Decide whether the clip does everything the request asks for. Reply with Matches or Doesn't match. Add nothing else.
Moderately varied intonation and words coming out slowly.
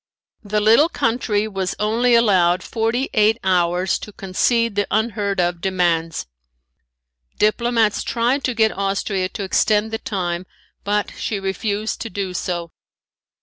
Matches